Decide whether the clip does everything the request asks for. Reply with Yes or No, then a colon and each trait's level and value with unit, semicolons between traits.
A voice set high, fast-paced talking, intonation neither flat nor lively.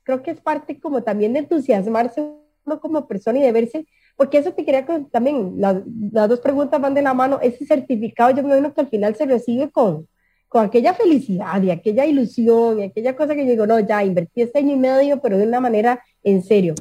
Yes: very high, 255 Hz; fast, 230 wpm; average, 4.9 semitones